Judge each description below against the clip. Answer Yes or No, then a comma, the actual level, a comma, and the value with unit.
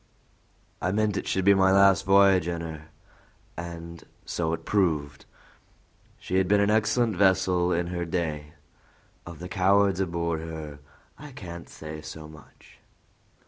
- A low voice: Yes, very low, 90 Hz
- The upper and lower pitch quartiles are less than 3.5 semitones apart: Yes, average, 3.1 semitones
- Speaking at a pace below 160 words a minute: Yes, average, 145 wpm